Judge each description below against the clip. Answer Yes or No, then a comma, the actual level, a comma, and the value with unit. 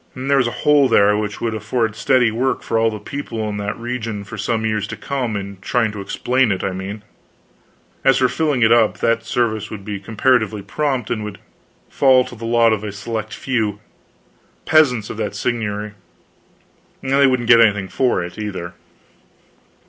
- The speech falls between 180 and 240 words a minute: Yes, average, 185 wpm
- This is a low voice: Yes, low, 110 Hz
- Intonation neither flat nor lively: Yes, average, 3.2 semitones